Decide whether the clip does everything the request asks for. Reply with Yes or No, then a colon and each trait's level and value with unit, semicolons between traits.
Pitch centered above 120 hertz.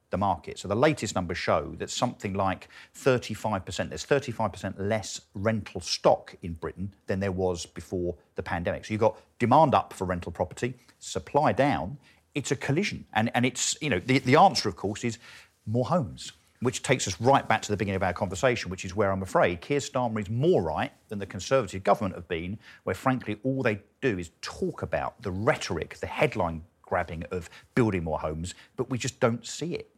No: low, 105 Hz